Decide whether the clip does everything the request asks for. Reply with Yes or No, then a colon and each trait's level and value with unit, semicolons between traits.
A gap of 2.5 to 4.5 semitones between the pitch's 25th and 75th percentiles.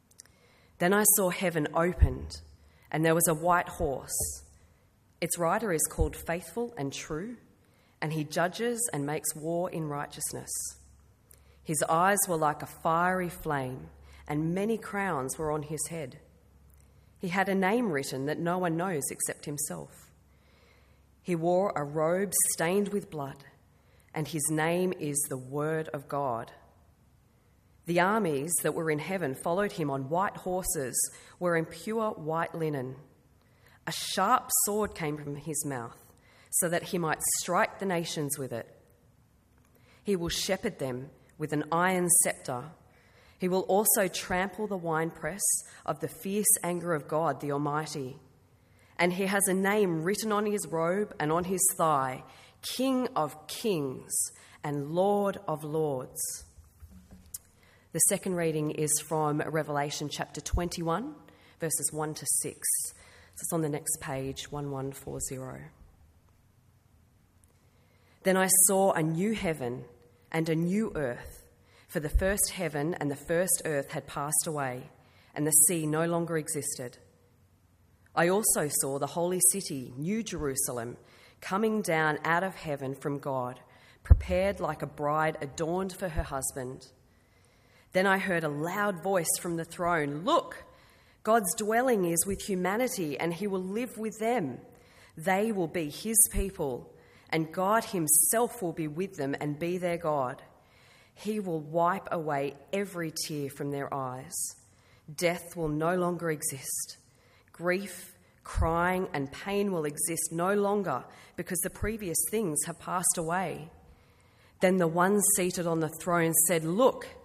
No: average, 5.2 semitones